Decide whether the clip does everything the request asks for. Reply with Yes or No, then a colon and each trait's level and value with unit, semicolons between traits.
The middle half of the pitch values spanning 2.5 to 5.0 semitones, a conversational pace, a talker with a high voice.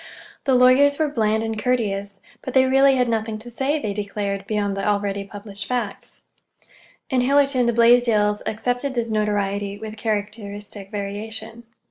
Yes: average, 3.4 semitones; average, 150 wpm; high, 220 Hz